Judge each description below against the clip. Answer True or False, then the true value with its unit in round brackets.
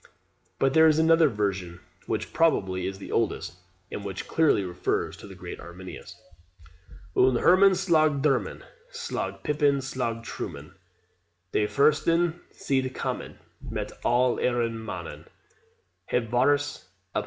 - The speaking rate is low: True (130 wpm)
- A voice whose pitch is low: True (130 Hz)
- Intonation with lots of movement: True (8.0 semitones)